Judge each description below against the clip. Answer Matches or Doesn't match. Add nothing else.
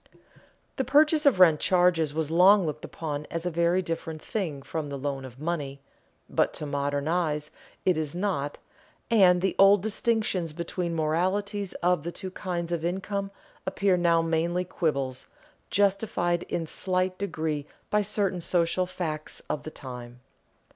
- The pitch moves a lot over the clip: Doesn't match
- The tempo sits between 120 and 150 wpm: Doesn't match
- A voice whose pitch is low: Doesn't match